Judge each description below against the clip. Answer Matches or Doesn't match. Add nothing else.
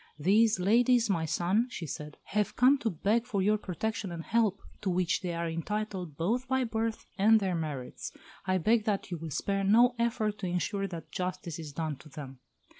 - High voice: Matches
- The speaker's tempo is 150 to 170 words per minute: Doesn't match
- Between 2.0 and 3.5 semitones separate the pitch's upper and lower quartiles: Doesn't match